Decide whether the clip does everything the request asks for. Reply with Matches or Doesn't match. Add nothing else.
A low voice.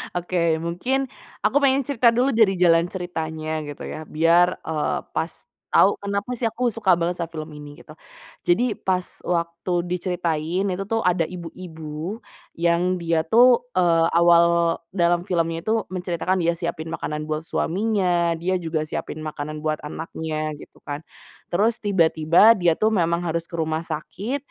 Doesn't match